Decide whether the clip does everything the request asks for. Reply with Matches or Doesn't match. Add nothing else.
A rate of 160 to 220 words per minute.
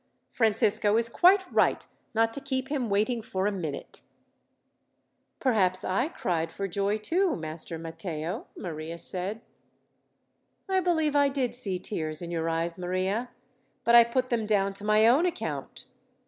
Doesn't match